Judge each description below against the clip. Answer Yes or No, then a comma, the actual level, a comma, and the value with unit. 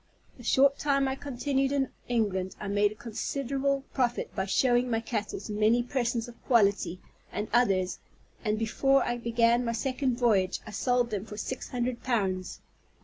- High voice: Yes, high, 240 Hz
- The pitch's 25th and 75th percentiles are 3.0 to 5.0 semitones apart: Yes, average, 3.6 semitones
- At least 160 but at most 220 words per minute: Yes, average, 170 wpm